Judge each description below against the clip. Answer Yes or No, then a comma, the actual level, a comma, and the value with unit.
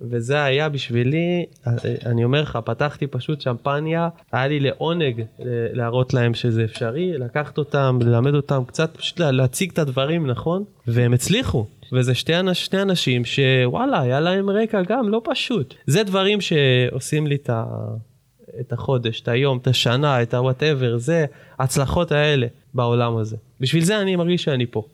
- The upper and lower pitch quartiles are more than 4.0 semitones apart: Yes, average, 4.8 semitones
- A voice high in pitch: No, low, 135 Hz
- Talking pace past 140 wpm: Yes, fast, 150 wpm